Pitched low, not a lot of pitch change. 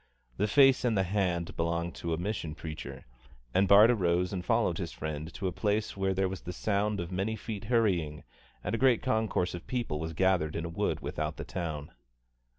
No: very low, 95 Hz; average, 4.1 semitones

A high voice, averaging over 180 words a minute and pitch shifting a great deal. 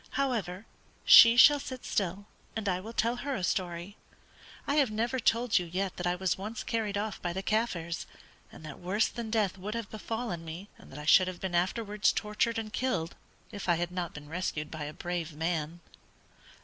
No: high, 195 Hz; average, 200 wpm; average, 4.4 semitones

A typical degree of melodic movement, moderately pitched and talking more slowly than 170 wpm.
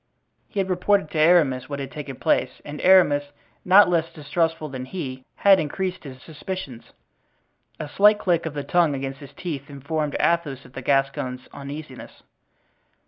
Yes: average, 4.3 semitones; medium, 150 Hz; average, 160 wpm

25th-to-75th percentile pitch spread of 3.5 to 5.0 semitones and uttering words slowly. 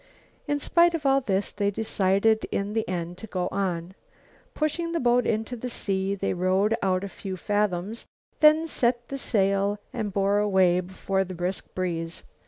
No: average, 4.0 semitones; average, 175 wpm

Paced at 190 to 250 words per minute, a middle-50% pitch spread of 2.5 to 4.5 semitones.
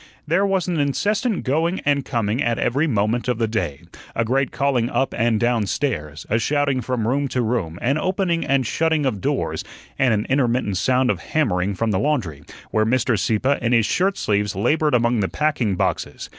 No: average, 195 wpm; average, 4.9 semitones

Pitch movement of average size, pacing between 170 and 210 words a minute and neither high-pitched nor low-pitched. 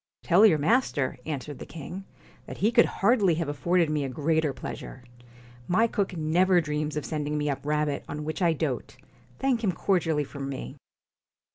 Yes: average, 3.8 semitones; average, 175 wpm; medium, 155 Hz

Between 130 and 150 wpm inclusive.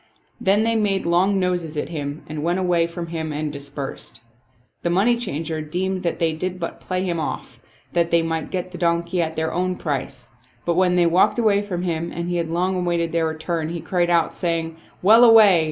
No: fast, 205 wpm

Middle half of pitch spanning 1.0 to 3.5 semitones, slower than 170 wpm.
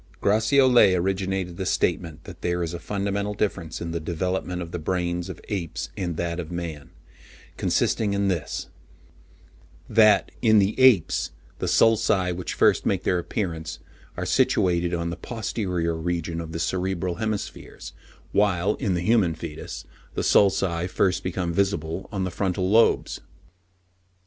Yes: average, 2.9 semitones; average, 145 wpm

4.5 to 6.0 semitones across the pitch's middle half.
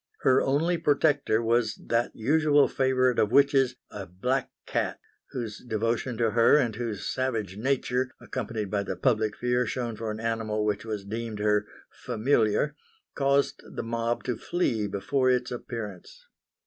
No: average, 3.3 semitones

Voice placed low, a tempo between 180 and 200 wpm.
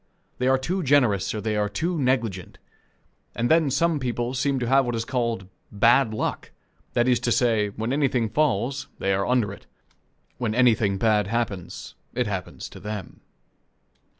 No: low, 120 Hz; average, 170 wpm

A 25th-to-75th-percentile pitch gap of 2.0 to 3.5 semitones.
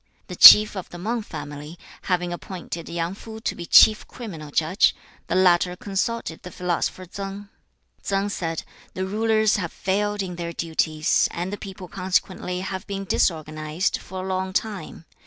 Yes: average, 2.8 semitones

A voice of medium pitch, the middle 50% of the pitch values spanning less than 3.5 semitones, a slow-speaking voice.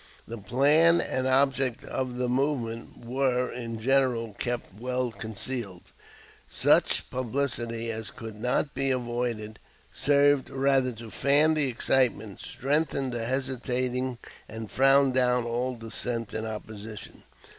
No: low, 125 Hz; narrow, 2.6 semitones; slow, 125 wpm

